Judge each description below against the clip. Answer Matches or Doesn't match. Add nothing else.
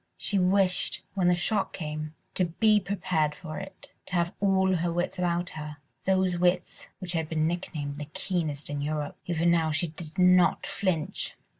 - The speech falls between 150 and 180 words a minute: Matches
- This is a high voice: Doesn't match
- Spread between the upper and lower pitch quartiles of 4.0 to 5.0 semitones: Doesn't match